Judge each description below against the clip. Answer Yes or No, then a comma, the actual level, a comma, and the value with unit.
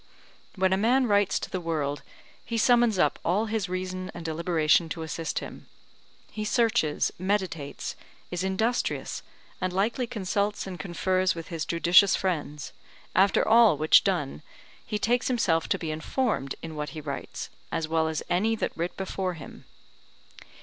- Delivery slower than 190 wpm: Yes, average, 155 wpm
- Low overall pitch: No, medium, 185 Hz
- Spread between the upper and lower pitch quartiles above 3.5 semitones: Yes, average, 4.4 semitones